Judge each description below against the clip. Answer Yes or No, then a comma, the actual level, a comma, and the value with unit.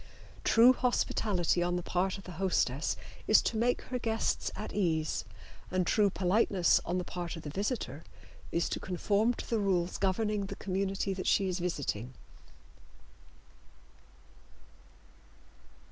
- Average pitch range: Yes, average, 3.2 semitones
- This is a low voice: No, high, 190 Hz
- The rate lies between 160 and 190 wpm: No, average, 140 wpm